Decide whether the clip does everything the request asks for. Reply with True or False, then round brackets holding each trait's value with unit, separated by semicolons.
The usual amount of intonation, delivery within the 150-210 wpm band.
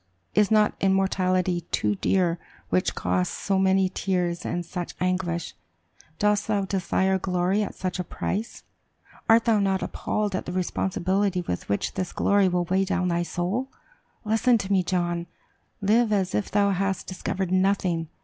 False (2.1 semitones; 160 wpm)